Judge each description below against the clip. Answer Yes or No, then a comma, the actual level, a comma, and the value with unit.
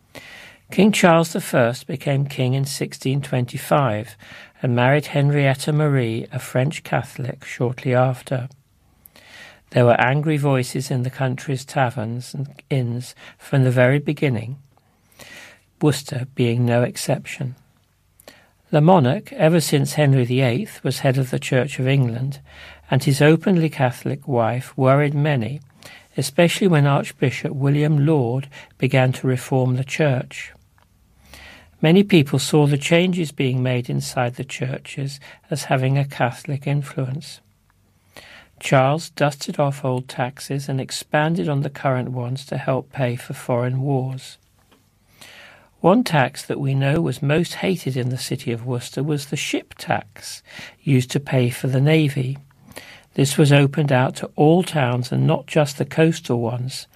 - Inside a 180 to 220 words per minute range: No, average, 140 wpm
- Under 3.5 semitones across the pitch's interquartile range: Yes, average, 2.9 semitones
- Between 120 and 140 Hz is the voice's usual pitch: Yes, low, 135 Hz